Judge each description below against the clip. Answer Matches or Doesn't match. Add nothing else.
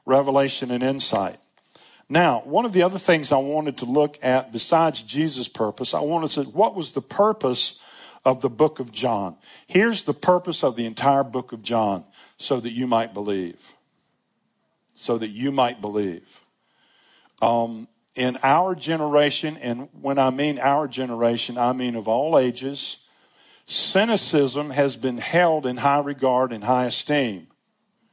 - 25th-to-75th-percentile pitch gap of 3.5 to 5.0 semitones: Matches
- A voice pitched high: Doesn't match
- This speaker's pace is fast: Doesn't match